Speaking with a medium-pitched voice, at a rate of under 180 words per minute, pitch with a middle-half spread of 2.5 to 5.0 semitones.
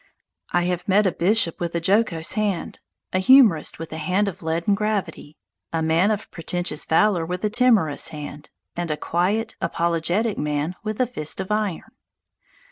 Yes: medium, 180 Hz; average, 170 wpm; average, 4.5 semitones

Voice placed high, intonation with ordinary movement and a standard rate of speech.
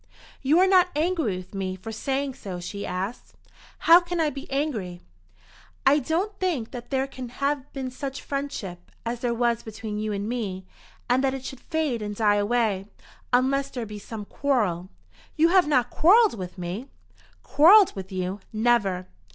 No: high, 245 Hz; wide, 5.7 semitones; average, 175 wpm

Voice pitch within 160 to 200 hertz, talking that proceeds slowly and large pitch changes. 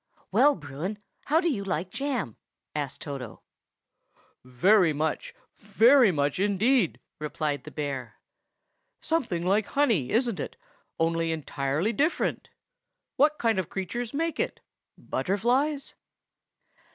Yes: high, 190 Hz; slow, 115 wpm; wide, 8.2 semitones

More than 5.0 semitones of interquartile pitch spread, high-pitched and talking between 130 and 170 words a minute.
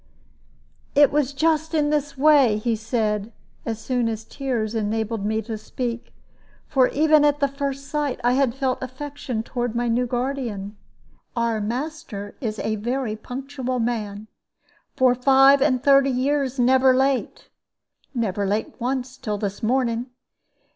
No: average, 3.7 semitones; very high, 250 Hz; average, 145 wpm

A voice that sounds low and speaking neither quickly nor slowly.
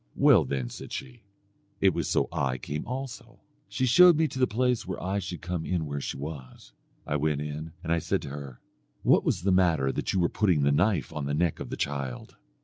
No: very low, 80 Hz; fast, 230 wpm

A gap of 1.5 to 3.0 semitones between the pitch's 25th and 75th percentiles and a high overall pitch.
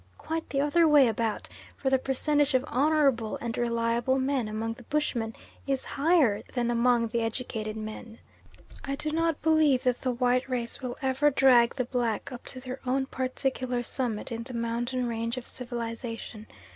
Yes: narrow, 2.6 semitones; very high, 250 Hz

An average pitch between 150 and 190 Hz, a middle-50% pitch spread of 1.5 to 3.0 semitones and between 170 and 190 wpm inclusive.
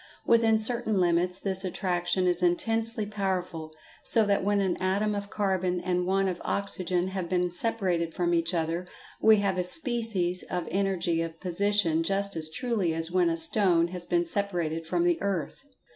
Yes: medium, 185 Hz; average, 2.7 semitones; average, 175 wpm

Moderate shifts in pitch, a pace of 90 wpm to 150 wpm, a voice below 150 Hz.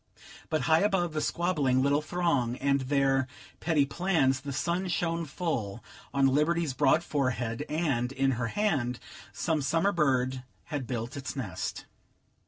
Yes: average, 4.2 semitones; average, 145 wpm; medium, 140 Hz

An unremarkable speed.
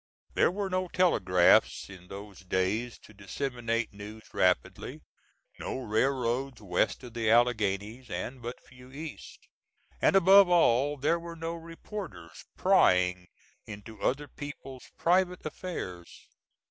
No: slow, 120 wpm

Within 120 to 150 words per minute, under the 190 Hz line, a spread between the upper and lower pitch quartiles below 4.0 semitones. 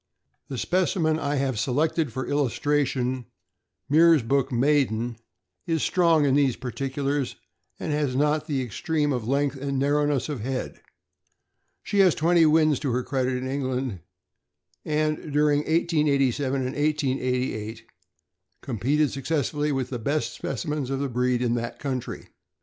Yes: average, 140 wpm; medium, 140 Hz; average, 2.9 semitones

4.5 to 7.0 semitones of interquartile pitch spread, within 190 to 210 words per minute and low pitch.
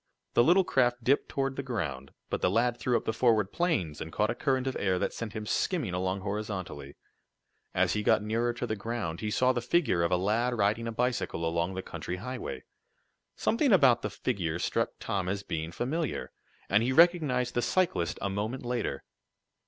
Yes: average, 5.1 semitones; average, 200 wpm; low, 115 Hz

